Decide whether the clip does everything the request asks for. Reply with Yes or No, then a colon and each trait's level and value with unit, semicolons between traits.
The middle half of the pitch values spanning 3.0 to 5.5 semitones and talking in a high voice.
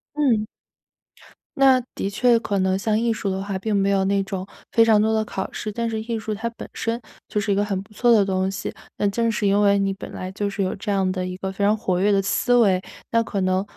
No: narrow, 2.4 semitones; high, 200 Hz